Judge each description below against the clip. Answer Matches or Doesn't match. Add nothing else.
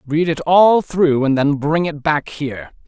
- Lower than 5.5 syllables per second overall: Matches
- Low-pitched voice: Doesn't match